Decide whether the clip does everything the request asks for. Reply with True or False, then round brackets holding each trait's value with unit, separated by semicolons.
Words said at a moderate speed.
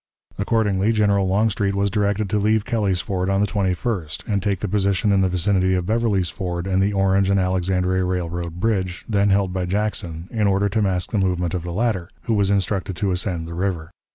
False (210 wpm)